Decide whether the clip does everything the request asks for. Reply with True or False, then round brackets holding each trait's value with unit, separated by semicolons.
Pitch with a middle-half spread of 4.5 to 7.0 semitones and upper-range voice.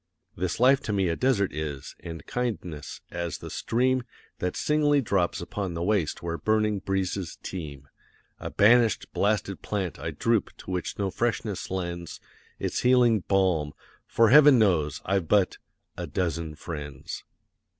False (4.8 semitones; 95 Hz)